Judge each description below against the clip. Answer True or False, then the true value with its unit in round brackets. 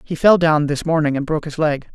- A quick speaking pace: True (280 wpm)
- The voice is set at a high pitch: False (155 Hz)